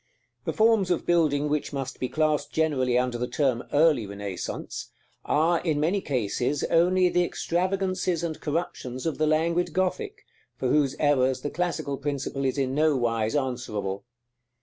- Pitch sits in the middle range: Yes, medium, 150 Hz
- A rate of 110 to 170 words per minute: Yes, average, 155 wpm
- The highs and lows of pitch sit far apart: No, average, 4.7 semitones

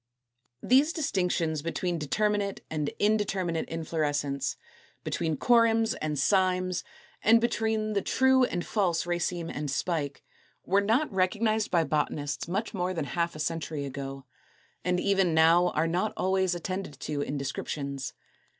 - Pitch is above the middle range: No, medium, 175 Hz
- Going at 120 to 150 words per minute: Yes, average, 140 wpm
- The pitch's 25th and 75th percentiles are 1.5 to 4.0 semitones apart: No, average, 5.0 semitones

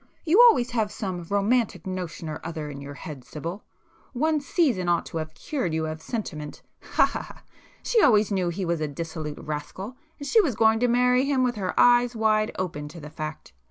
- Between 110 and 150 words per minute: No, average, 195 wpm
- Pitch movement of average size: No, wide, 7.5 semitones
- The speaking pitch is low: No, medium, 185 Hz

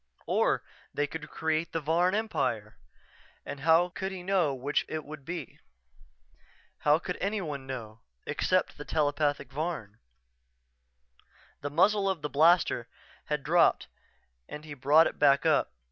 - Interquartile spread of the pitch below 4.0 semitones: Yes, average, 3.4 semitones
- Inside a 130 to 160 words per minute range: Yes, average, 140 wpm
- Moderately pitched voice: Yes, medium, 155 Hz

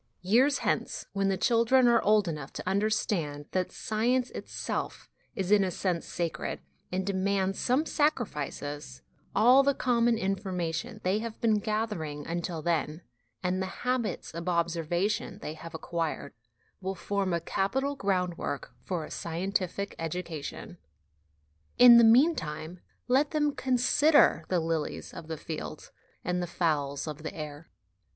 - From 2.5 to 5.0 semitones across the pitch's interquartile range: No, wide, 5.5 semitones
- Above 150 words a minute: No, average, 145 wpm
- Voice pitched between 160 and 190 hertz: Yes, medium, 185 Hz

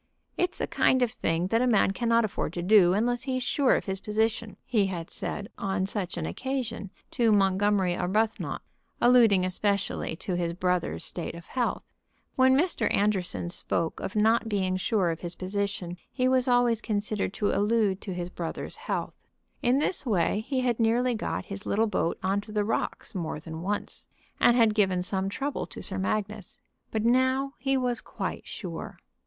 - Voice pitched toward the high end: Yes, high, 210 Hz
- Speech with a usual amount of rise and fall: Yes, average, 4.2 semitones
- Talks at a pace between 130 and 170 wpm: No, average, 180 wpm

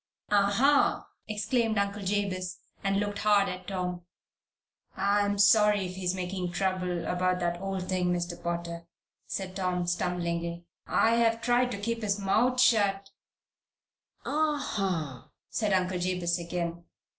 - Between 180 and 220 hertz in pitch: Yes, high, 190 Hz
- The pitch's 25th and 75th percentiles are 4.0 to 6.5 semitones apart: No, narrow, 2.6 semitones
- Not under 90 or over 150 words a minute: Yes, slow, 135 wpm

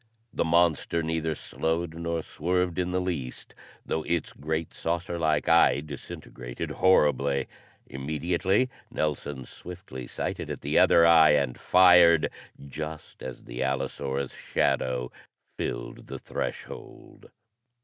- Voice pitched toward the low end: Yes, very low, 80 Hz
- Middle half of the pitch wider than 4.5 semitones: No, average, 3.5 semitones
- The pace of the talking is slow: Yes, slow, 120 wpm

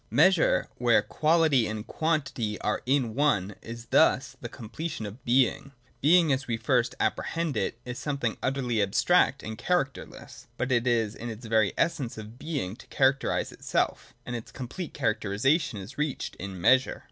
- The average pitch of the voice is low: Yes, low, 125 Hz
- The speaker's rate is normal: Yes, average, 160 wpm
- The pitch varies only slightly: No, average, 4.4 semitones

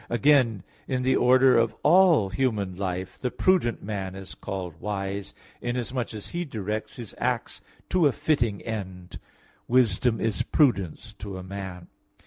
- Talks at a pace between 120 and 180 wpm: Yes, average, 150 wpm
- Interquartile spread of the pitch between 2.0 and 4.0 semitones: No, average, 4.8 semitones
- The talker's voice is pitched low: Yes, low, 110 Hz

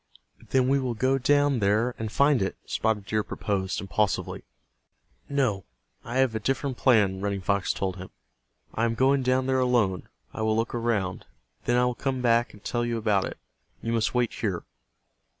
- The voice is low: Yes, low, 115 Hz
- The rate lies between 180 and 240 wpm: Yes, average, 185 wpm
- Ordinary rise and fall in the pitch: Yes, average, 3.9 semitones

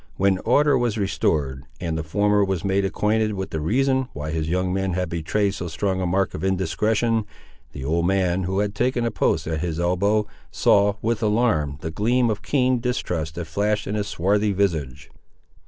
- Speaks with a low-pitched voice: Yes, very low, 95 Hz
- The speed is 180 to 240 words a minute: Yes, average, 190 wpm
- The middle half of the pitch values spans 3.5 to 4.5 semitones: Yes, average, 4.1 semitones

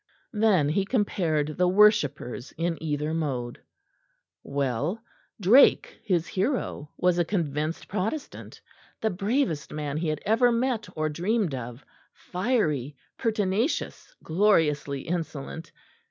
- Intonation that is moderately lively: No, wide, 6.0 semitones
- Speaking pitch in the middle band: Yes, medium, 170 Hz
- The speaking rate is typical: No, slow, 110 wpm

